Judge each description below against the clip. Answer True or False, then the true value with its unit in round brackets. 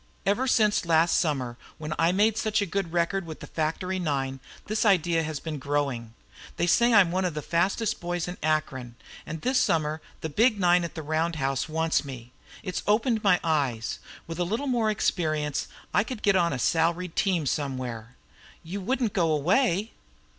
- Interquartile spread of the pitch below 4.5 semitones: False (4.8 semitones)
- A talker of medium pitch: True (170 Hz)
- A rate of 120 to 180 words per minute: False (190 wpm)